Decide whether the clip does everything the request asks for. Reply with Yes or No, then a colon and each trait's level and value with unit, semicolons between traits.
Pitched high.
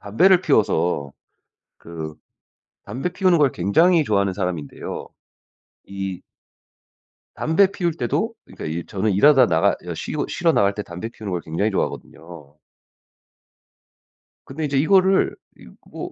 No: low, 105 Hz